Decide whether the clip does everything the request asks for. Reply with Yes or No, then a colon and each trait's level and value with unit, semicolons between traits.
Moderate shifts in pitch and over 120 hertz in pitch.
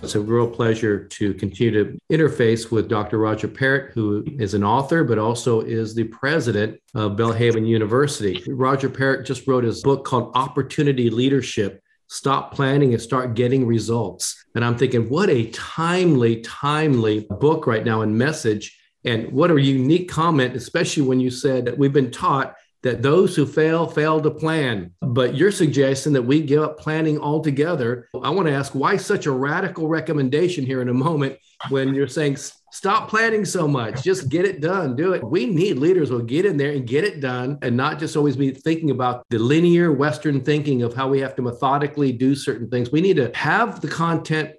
Yes: average, 4.4 semitones; low, 135 Hz